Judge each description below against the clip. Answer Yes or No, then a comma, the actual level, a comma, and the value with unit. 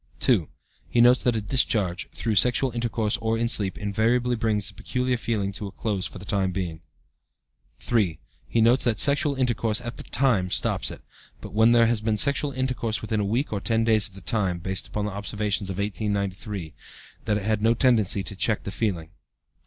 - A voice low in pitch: Yes, low, 110 Hz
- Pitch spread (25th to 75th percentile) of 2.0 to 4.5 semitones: Yes, average, 2.9 semitones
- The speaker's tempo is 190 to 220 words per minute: Yes, average, 200 wpm